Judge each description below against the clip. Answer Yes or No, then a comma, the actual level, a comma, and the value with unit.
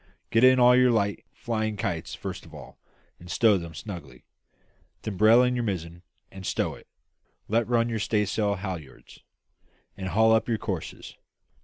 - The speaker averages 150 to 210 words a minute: Yes, average, 165 wpm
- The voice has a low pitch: Yes, low, 105 Hz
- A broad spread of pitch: No, average, 3.8 semitones